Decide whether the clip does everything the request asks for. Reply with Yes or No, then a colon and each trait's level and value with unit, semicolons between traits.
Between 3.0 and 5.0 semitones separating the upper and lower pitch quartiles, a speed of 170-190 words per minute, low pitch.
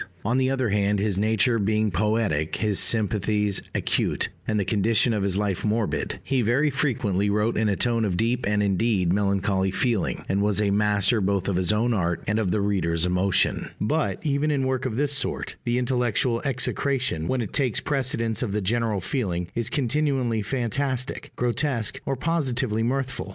Yes: average, 3.9 semitones; average, 180 wpm; low, 110 Hz